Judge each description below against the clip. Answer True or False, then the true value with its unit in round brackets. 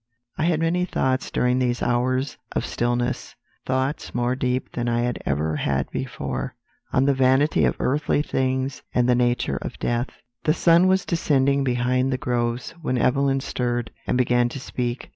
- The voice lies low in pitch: True (125 Hz)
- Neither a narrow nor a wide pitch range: False (2.0 semitones)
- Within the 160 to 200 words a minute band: True (170 wpm)